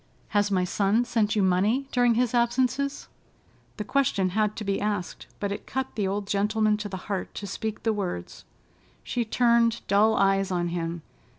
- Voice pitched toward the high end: Yes, high, 210 Hz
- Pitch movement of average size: Yes, average, 3.1 semitones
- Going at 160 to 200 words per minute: Yes, average, 180 wpm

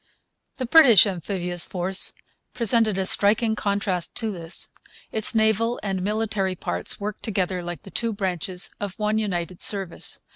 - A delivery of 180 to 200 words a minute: No, average, 145 wpm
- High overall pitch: Yes, high, 200 Hz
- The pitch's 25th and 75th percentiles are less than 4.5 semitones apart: Yes, average, 3.1 semitones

